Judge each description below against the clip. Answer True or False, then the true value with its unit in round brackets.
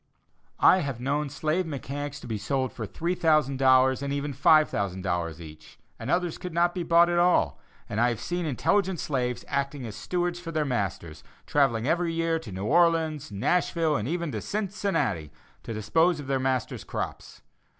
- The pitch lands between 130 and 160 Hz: True (140 Hz)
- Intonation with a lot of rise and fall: True (5.9 semitones)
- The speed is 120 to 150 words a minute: False (170 wpm)